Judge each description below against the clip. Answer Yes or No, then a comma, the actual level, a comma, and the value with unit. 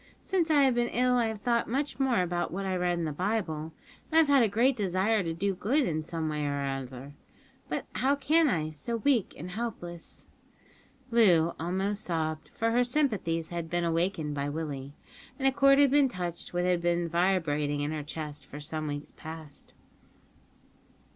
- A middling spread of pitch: No, wide, 6.9 semitones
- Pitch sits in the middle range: Yes, medium, 175 Hz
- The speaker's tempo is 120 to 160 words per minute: No, average, 190 wpm